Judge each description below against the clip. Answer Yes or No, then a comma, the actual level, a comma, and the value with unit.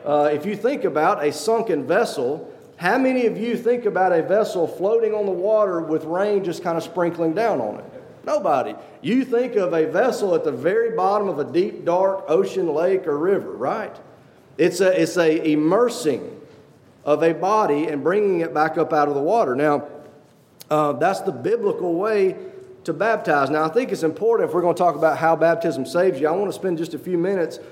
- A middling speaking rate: No, fast, 210 wpm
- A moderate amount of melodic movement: No, wide, 6.2 semitones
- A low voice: No, medium, 180 Hz